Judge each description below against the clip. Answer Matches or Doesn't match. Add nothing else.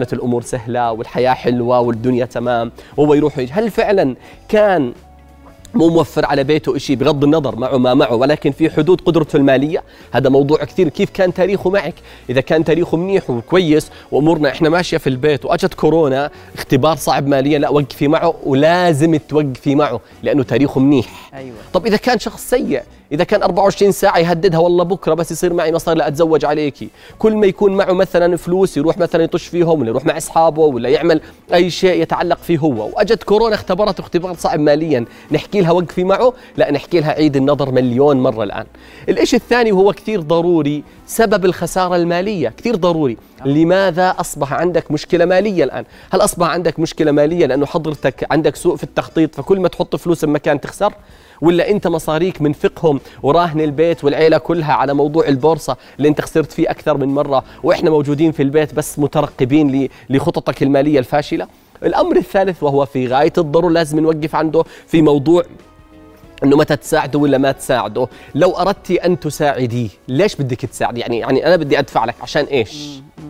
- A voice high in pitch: Doesn't match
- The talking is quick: Matches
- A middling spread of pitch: Matches